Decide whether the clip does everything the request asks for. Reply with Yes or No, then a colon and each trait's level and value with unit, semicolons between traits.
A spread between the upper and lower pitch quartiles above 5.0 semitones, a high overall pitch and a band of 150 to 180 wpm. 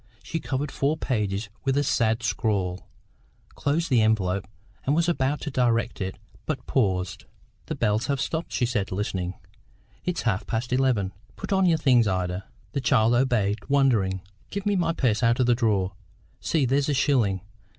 No: wide, 5.6 semitones; low, 120 Hz; average, 170 wpm